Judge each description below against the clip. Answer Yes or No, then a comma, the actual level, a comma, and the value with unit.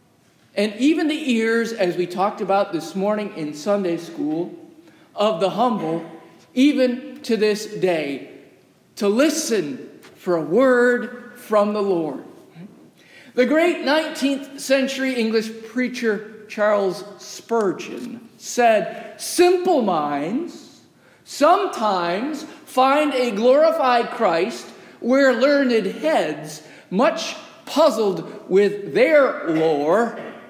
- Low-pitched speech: No, high, 235 Hz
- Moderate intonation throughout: No, wide, 5.9 semitones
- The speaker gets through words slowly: Yes, slow, 100 wpm